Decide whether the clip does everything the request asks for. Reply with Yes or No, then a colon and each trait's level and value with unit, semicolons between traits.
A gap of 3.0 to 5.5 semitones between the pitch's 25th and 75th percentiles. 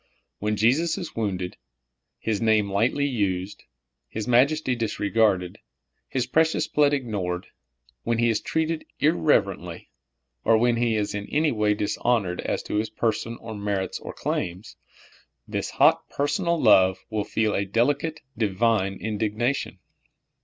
Yes: average, 3.9 semitones